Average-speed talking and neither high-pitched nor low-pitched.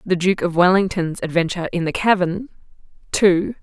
Yes: average, 150 wpm; medium, 180 Hz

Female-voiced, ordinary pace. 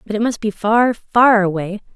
No: female; fast, 215 wpm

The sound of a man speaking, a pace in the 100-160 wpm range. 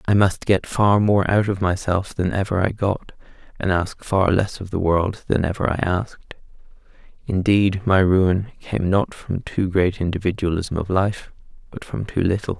No: male; average, 180 wpm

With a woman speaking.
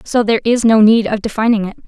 Yes: female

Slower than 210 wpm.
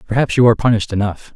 No: fast, 220 wpm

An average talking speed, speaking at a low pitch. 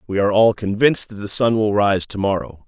No: fast, 245 wpm; low, 105 Hz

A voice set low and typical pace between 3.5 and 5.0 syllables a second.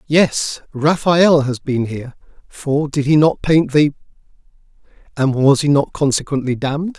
No: medium, 145 Hz; 4.6 syllables/s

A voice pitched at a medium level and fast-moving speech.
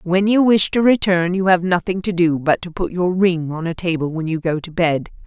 Yes: medium, 175 Hz; fast, 260 wpm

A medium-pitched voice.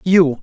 Yes: medium, 165 Hz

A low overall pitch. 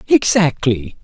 No: medium, 170 Hz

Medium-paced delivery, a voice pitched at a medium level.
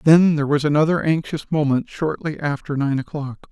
Yes: average, 170 wpm; medium, 150 Hz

